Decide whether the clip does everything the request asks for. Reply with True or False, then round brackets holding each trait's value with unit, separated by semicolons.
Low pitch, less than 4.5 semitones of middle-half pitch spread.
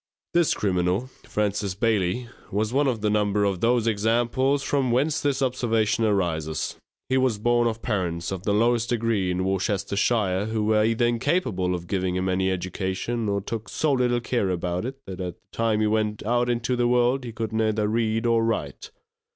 True (110 Hz; 3.8 semitones)